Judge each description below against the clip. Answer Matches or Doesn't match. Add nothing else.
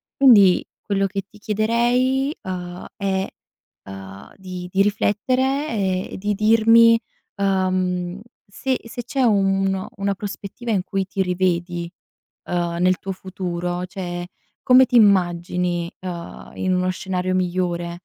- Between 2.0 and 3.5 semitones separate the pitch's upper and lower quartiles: Matches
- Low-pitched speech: Doesn't match